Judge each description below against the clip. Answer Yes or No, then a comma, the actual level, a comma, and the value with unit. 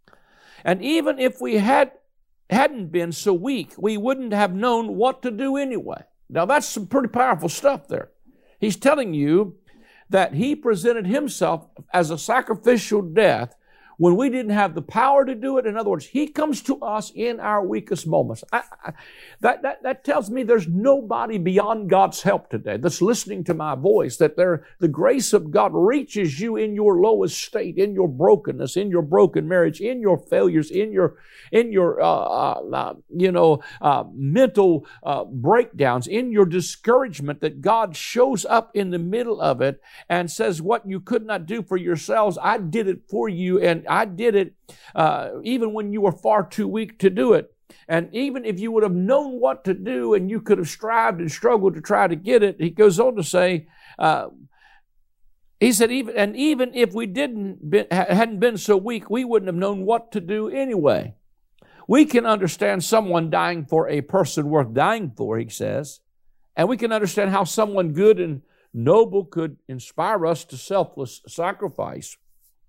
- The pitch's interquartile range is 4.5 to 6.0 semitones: Yes, average, 5.0 semitones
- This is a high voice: Yes, high, 205 Hz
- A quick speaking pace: No, average, 185 wpm